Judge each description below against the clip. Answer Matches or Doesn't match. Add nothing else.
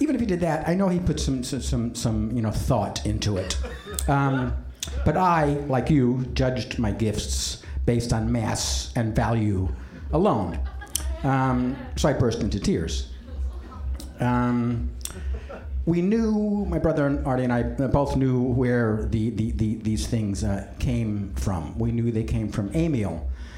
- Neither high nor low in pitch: Doesn't match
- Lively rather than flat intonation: Matches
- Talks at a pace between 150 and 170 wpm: Matches